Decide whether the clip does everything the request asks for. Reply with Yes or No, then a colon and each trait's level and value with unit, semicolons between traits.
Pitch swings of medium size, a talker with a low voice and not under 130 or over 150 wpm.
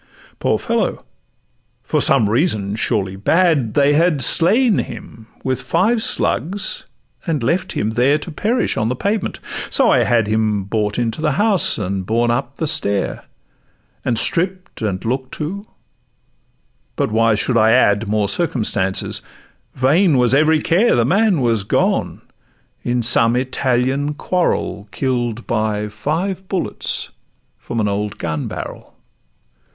No: wide, 7.3 semitones; low, 125 Hz; slow, 135 wpm